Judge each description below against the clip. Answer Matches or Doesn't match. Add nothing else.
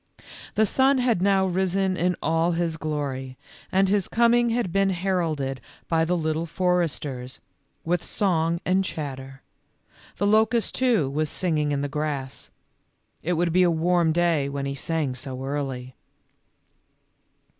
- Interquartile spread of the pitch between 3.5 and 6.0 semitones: Matches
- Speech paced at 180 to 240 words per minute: Doesn't match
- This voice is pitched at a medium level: Matches